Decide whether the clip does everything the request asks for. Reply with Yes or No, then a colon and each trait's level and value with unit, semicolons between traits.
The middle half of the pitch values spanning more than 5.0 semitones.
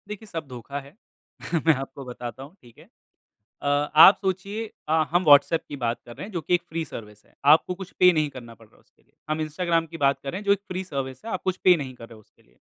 Yes: wide, 5.6 semitones